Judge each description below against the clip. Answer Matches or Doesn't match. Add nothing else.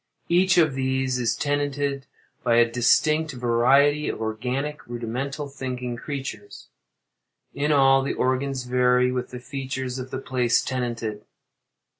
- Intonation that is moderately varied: Doesn't match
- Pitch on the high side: Doesn't match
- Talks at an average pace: Doesn't match